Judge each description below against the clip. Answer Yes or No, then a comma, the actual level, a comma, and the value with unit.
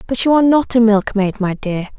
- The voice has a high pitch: Yes, high, 225 Hz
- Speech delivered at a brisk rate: Yes, fast, 240 wpm